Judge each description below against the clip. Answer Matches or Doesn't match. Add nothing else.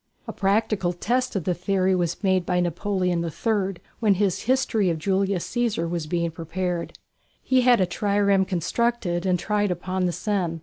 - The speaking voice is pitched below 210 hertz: Matches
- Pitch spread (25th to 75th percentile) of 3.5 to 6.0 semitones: Doesn't match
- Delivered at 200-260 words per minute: Doesn't match